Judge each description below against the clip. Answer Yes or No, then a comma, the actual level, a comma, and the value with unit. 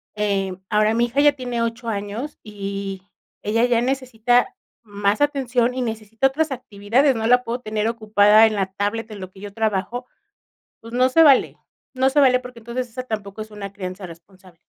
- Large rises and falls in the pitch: No, average, 3.6 semitones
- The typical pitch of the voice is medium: No, high, 225 Hz